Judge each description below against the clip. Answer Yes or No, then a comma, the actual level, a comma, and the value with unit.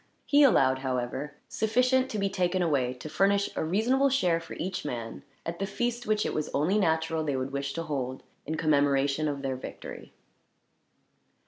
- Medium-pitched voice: Yes, medium, 160 Hz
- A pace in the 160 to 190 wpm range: Yes, average, 180 wpm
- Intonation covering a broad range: Yes, wide, 6.4 semitones